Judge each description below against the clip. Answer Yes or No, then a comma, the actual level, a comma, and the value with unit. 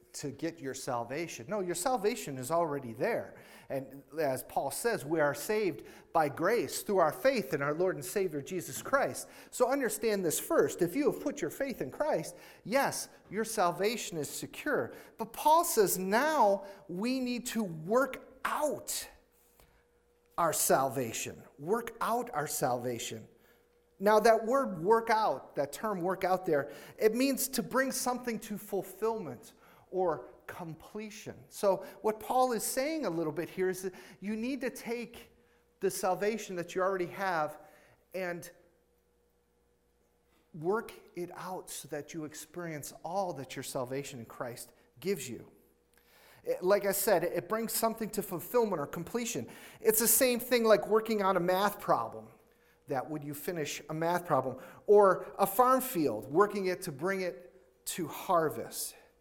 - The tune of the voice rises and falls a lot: Yes, wide, 6.9 semitones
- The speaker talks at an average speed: Yes, average, 155 wpm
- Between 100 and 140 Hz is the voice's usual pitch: No, medium, 185 Hz